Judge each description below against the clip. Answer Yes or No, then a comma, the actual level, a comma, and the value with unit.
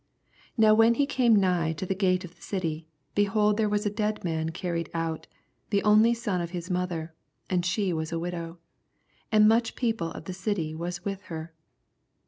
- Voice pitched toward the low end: No, medium, 185 Hz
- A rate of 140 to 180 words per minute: No, average, 195 wpm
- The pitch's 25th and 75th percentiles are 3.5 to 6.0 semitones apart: Yes, average, 4.0 semitones